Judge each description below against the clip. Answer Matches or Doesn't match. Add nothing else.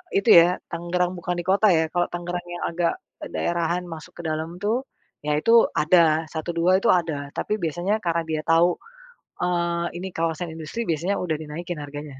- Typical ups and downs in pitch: Doesn't match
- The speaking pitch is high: Doesn't match